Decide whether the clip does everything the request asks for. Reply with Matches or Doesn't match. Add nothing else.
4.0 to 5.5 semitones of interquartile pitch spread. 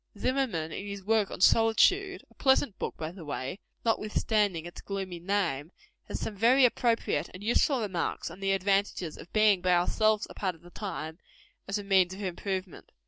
Doesn't match